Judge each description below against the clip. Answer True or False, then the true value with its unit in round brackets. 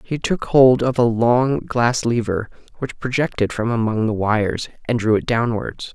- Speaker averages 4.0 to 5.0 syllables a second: True (4.4 syllables/s)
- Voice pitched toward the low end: True (120 Hz)